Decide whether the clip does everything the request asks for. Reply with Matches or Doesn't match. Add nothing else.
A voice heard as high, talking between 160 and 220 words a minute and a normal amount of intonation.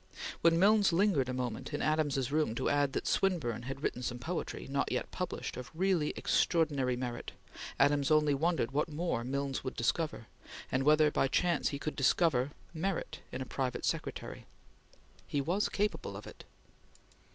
Doesn't match